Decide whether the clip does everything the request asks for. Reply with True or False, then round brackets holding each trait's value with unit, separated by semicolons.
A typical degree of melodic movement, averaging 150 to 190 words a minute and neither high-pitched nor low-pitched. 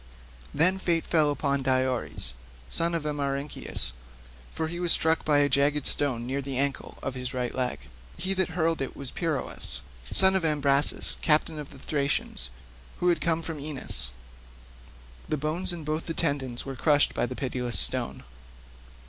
True (3.4 semitones; 165 wpm; 145 Hz)